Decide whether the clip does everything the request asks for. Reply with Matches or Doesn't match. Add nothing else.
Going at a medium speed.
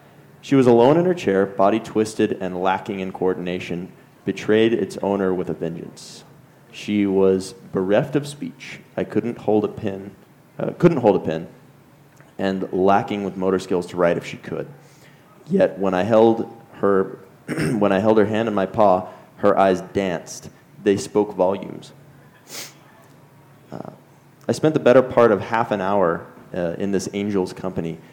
Matches